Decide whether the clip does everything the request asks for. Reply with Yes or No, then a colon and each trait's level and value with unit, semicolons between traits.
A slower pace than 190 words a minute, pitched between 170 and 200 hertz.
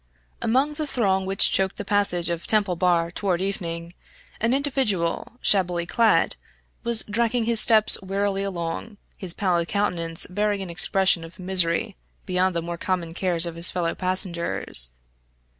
Yes: average, 150 wpm; medium, 185 Hz